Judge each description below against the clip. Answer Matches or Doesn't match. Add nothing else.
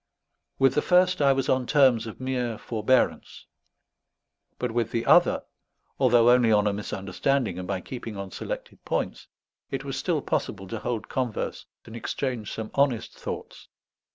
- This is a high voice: Doesn't match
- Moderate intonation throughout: Matches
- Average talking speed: Matches